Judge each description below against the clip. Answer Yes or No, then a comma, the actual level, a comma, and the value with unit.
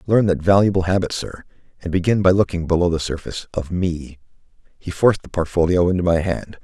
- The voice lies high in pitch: No, very low, 90 Hz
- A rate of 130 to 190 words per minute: Yes, average, 180 wpm